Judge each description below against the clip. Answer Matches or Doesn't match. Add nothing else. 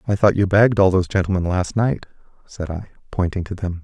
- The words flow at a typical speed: Doesn't match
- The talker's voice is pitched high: Doesn't match